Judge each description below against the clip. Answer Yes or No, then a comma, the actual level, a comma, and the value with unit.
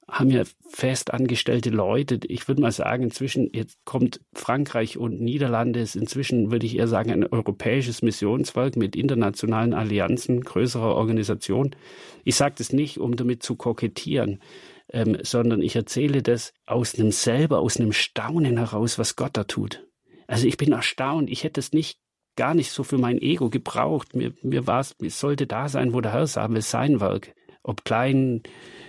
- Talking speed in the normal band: Yes, average, 175 wpm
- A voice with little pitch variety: No, average, 3.0 semitones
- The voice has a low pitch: Yes, low, 120 Hz